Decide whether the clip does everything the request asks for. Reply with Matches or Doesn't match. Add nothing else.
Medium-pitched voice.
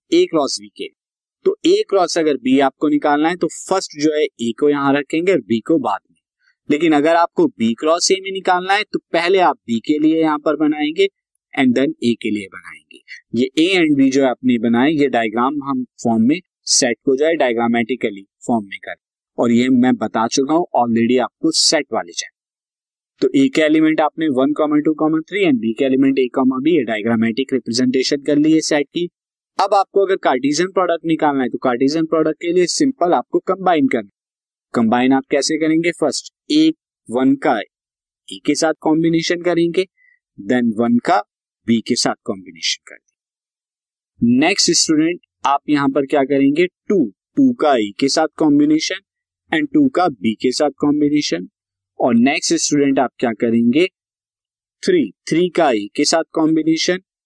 Matches